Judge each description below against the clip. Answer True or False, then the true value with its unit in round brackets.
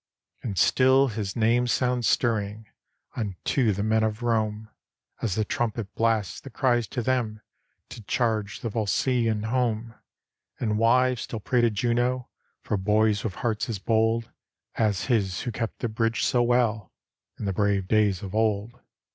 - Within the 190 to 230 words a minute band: False (155 wpm)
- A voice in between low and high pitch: False (110 Hz)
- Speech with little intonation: True (2.2 semitones)